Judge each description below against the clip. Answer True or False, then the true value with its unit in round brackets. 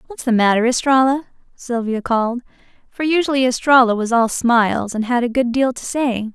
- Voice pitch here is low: False (245 Hz)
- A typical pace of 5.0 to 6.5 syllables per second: True (5.5 syllables/s)